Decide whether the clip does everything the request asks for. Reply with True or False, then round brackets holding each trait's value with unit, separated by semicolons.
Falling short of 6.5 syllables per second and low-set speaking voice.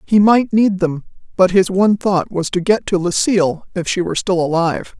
False (5.4 syllables/s; 185 Hz)